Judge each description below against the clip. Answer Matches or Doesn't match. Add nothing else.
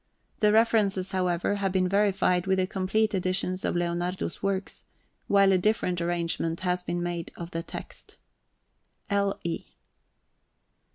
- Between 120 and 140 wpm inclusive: Matches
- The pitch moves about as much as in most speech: Doesn't match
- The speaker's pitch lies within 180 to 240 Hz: Matches